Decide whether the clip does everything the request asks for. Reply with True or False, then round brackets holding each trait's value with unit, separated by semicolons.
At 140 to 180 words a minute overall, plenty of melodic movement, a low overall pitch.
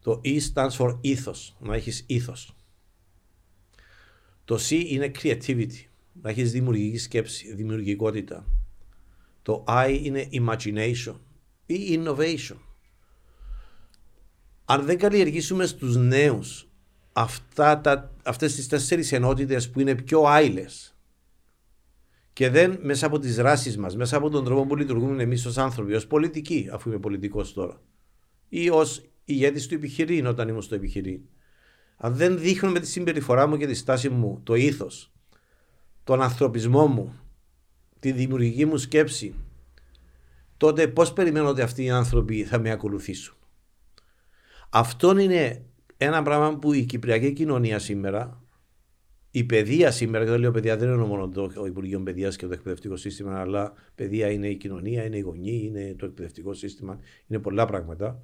True (145 wpm; 5.7 semitones; 120 Hz)